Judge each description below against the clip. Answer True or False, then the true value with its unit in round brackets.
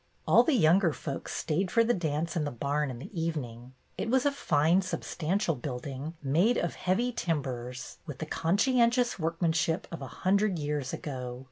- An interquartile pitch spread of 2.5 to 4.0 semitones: False (5.3 semitones)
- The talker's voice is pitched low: False (160 Hz)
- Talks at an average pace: True (175 wpm)